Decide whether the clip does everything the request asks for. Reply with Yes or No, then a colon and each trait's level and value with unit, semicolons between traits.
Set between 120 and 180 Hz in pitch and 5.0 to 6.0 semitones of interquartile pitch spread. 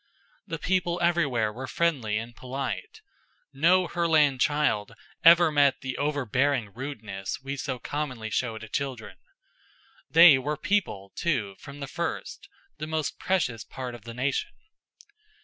Yes: medium, 140 Hz; average, 5.3 semitones